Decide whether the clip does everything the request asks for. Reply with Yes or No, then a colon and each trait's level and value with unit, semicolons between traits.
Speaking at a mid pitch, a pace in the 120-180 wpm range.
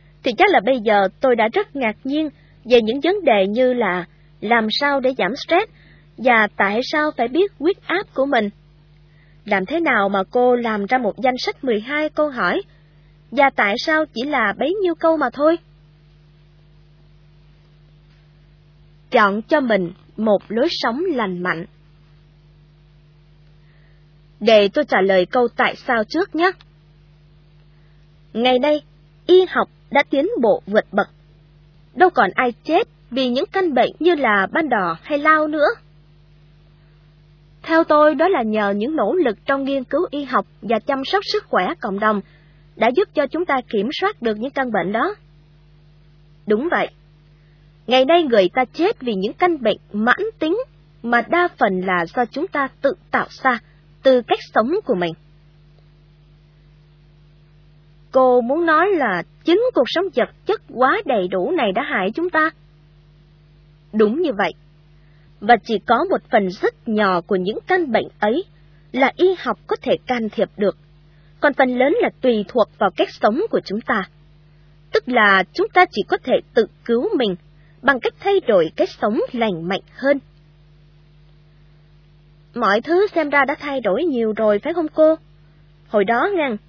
No: high, 210 Hz; slow, 165 wpm